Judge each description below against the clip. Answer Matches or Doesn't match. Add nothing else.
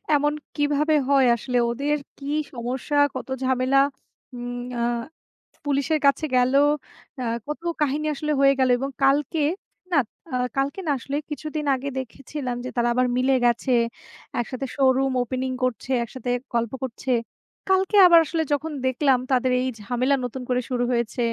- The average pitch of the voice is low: Doesn't match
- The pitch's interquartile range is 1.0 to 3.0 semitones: Matches